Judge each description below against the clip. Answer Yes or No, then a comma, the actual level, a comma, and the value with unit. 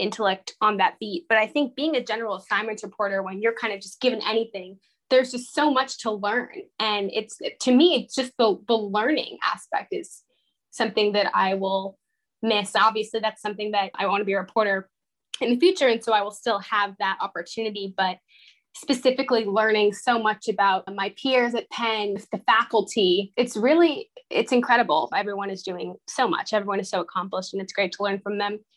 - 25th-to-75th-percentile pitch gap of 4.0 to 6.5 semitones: No, average, 3.3 semitones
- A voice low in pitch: No, high, 215 Hz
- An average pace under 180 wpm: No, average, 195 wpm